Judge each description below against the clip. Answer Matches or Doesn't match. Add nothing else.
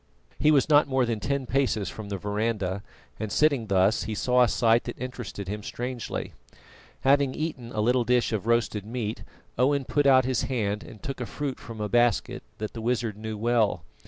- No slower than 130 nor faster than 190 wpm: Doesn't match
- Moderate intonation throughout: Matches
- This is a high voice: Doesn't match